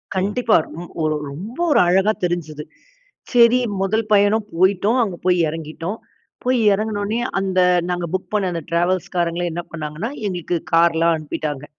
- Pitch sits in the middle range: Yes, medium, 180 Hz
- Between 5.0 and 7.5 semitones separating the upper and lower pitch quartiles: No, average, 3.7 semitones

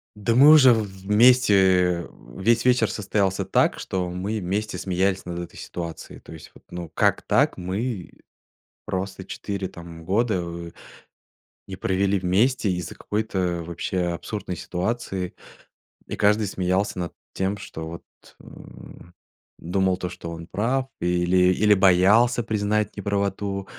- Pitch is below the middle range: Yes, very low, 95 Hz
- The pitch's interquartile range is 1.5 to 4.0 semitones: Yes, average, 3.0 semitones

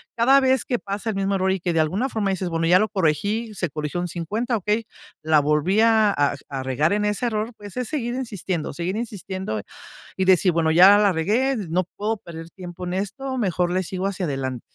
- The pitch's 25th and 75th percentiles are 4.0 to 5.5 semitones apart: Yes, average, 4.5 semitones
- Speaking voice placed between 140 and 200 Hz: Yes, high, 190 Hz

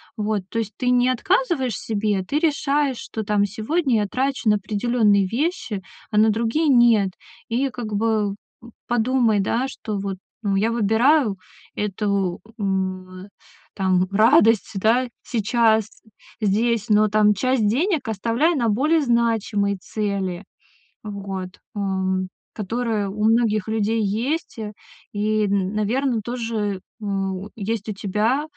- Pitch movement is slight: No, average, 3.1 semitones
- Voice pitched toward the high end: Yes, high, 215 Hz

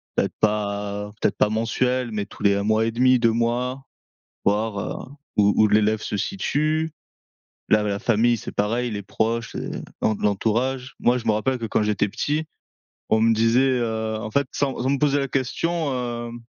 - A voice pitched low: Yes, low, 115 Hz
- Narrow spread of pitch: No, average, 3.3 semitones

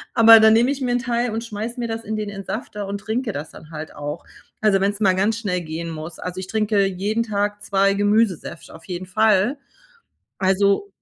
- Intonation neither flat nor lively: Yes, average, 3.0 semitones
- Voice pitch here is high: Yes, high, 205 Hz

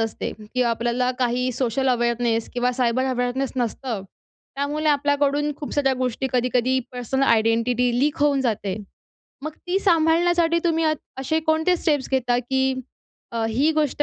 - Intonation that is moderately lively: Yes, average, 3.3 semitones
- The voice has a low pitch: No, very high, 260 Hz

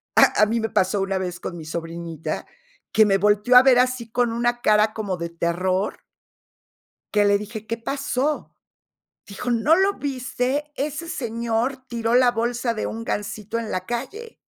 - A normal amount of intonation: Yes, average, 3.7 semitones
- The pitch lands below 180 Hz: No, high, 230 Hz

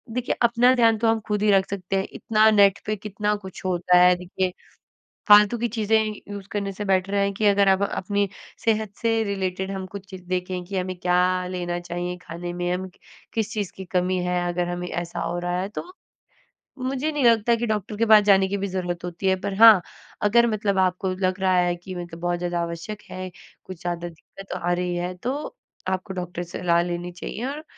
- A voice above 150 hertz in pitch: Yes, high, 190 Hz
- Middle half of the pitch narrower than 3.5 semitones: Yes, average, 2.8 semitones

